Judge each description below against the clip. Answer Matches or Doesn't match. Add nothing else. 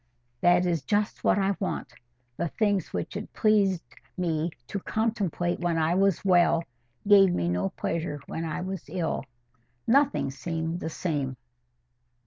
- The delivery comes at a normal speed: Matches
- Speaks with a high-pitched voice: Doesn't match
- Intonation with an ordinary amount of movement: Matches